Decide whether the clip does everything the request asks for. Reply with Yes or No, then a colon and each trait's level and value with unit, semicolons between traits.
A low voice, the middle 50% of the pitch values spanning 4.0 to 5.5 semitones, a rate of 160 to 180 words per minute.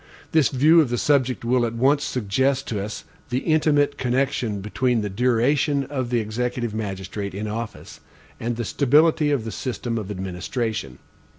Yes: low, 120 Hz; average, 4.3 semitones; average, 165 wpm